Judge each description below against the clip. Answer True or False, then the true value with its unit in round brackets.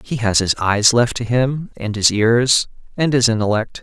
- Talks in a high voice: False (115 Hz)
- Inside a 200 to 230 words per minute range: True (205 wpm)